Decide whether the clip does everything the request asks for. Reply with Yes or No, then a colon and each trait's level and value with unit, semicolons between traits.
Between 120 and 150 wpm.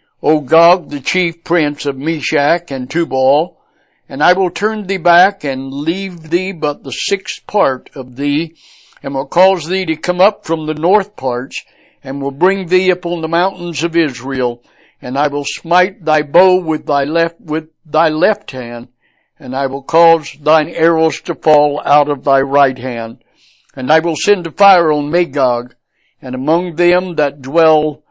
No: average, 175 wpm